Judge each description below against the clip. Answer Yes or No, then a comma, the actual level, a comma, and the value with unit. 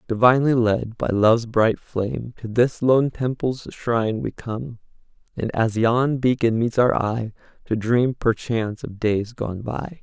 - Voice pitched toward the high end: No, low, 115 Hz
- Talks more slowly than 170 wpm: Yes, average, 160 wpm